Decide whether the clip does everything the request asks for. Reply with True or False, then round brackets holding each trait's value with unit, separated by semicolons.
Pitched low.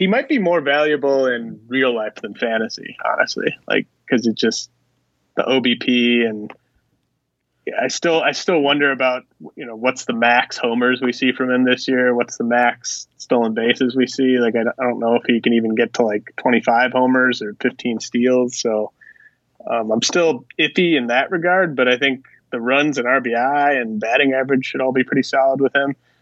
True (125 Hz)